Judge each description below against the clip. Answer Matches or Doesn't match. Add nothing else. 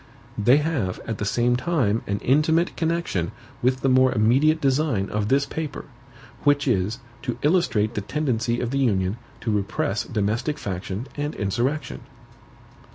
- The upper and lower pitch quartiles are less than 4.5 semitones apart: Doesn't match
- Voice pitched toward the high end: Doesn't match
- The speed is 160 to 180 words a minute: Doesn't match